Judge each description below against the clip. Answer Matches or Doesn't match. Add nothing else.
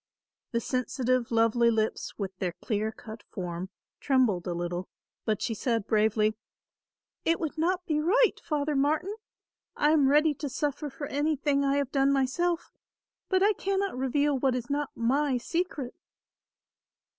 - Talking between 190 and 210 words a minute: Doesn't match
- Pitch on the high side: Matches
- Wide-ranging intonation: Doesn't match